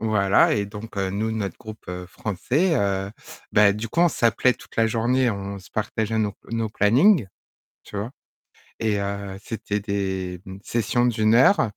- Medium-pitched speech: No, low, 105 Hz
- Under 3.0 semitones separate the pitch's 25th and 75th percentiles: Yes, narrow, 2.4 semitones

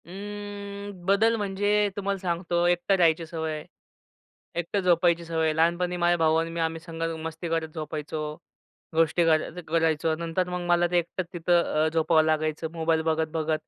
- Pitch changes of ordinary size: No, narrow, 1.9 semitones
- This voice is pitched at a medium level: Yes, medium, 170 Hz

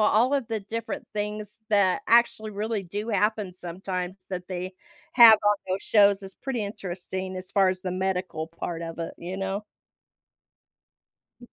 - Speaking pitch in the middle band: No, high, 195 Hz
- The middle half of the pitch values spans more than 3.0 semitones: No, narrow, 2.6 semitones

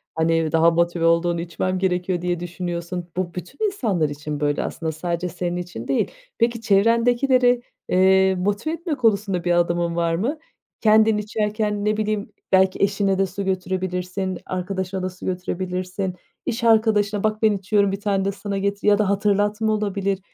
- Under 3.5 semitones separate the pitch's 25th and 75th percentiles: Yes, average, 3.0 semitones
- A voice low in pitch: No, high, 190 Hz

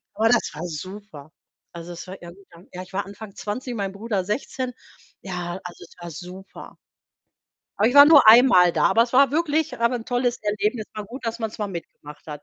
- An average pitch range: Yes, average, 5.0 semitones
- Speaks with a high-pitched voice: Yes, high, 205 Hz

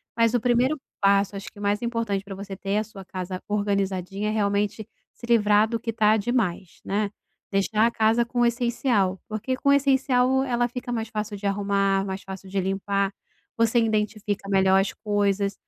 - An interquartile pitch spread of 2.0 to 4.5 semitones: Yes, average, 2.8 semitones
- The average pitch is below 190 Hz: No, high, 210 Hz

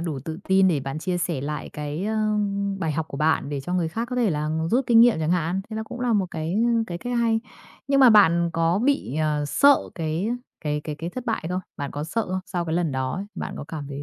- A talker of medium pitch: Yes, medium, 170 Hz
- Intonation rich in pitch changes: Yes, wide, 6.0 semitones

